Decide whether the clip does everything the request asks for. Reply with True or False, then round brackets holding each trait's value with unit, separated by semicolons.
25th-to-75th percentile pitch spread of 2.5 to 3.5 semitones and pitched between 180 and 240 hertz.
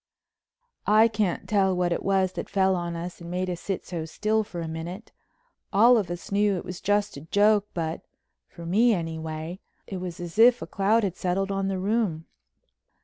True (3.1 semitones; 190 Hz)